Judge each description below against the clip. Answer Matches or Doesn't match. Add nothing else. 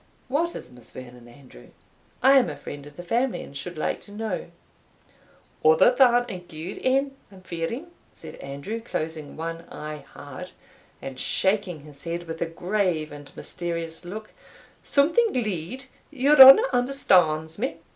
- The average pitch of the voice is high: Doesn't match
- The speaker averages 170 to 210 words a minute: Doesn't match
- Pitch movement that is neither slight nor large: Doesn't match